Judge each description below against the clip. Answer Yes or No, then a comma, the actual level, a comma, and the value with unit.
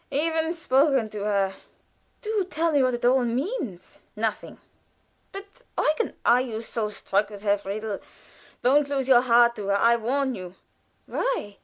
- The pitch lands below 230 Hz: No, high, 240 Hz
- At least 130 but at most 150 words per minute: No, average, 165 wpm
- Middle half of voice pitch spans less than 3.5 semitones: No, average, 5.2 semitones